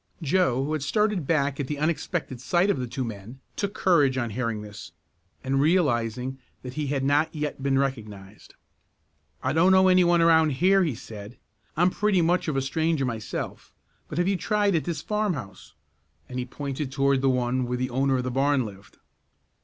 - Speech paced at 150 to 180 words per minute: No, average, 195 wpm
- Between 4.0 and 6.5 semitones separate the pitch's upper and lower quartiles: Yes, average, 5.0 semitones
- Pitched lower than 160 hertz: Yes, medium, 140 Hz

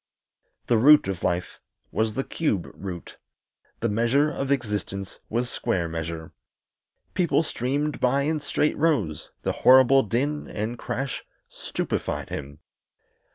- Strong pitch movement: Yes, wide, 6.3 semitones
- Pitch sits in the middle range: No, low, 120 Hz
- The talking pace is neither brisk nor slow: No, slow, 125 wpm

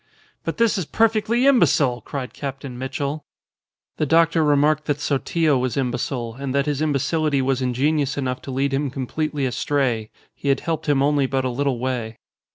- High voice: No, medium, 140 Hz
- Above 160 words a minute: Yes, average, 175 wpm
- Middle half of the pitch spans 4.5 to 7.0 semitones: No, average, 2.8 semitones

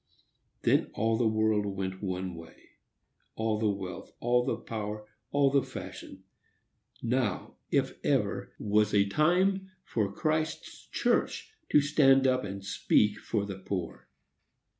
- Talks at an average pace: No, slow, 130 wpm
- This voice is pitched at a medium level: No, low, 110 Hz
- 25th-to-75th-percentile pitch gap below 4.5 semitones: No, average, 5.0 semitones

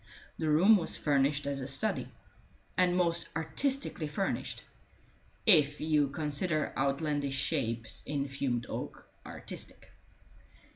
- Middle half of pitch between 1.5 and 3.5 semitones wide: Yes, average, 3.2 semitones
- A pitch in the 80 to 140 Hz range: No, medium, 150 Hz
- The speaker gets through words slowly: Yes, slow, 110 wpm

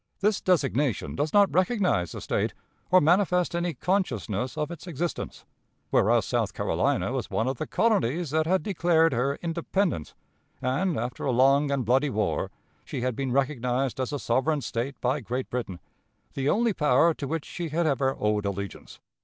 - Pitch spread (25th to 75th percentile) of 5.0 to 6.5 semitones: Yes, wide, 5.4 semitones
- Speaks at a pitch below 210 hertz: Yes, medium, 140 Hz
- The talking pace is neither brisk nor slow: Yes, average, 170 wpm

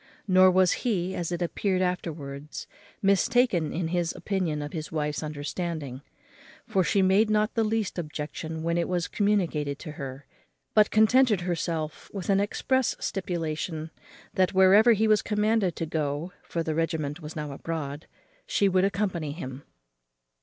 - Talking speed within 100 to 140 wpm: No, average, 155 wpm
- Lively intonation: No, average, 4.2 semitones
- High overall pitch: No, medium, 175 Hz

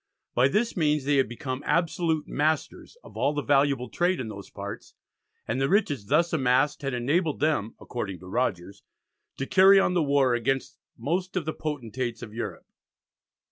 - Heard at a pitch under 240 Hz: Yes, medium, 140 Hz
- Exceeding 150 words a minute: Yes, average, 175 wpm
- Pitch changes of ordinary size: Yes, average, 4.6 semitones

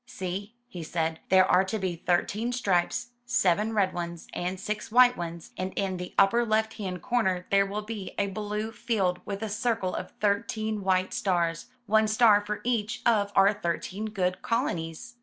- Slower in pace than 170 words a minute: No, average, 175 wpm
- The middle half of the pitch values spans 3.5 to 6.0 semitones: No, average, 3.1 semitones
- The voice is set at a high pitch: Yes, high, 200 Hz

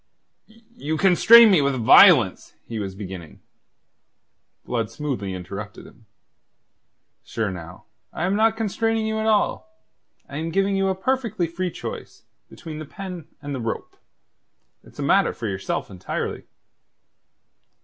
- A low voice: No, medium, 155 Hz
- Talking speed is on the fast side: No, slow, 135 wpm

